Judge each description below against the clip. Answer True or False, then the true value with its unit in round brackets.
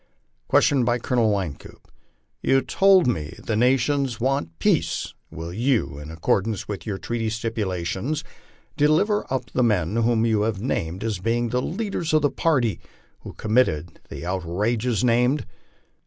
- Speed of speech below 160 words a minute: True (145 wpm)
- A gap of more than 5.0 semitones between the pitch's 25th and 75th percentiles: True (5.5 semitones)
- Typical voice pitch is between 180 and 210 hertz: False (115 Hz)